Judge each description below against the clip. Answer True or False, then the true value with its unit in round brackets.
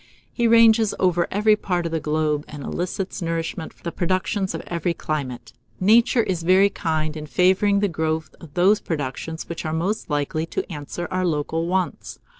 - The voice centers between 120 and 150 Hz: False (170 Hz)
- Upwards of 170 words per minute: True (180 wpm)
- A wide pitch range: False (3.3 semitones)